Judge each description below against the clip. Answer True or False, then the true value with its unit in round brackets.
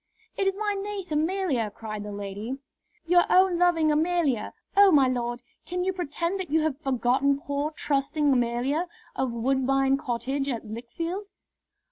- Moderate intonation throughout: False (6.1 semitones)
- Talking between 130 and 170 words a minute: True (150 wpm)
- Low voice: False (285 Hz)